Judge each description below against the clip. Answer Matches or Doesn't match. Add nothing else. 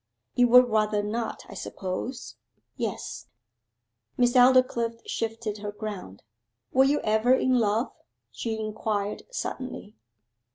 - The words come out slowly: Matches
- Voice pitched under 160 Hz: Doesn't match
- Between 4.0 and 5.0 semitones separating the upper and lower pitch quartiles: Doesn't match